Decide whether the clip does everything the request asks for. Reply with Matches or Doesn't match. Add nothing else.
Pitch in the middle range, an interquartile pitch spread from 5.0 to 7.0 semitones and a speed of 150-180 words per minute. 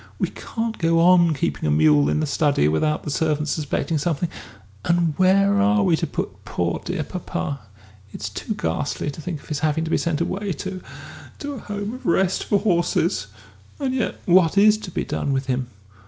Doesn't match